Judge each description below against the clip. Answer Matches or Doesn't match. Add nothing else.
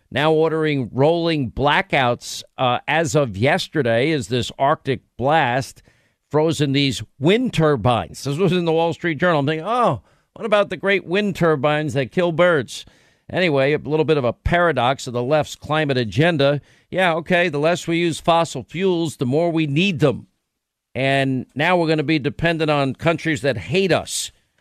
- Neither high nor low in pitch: Matches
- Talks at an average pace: Matches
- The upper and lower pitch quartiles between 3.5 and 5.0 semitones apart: Matches